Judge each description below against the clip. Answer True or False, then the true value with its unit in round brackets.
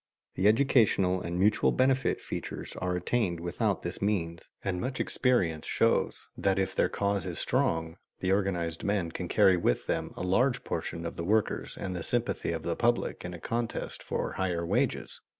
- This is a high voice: False (95 Hz)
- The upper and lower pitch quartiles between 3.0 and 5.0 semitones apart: True (4.2 semitones)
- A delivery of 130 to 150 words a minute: False (180 wpm)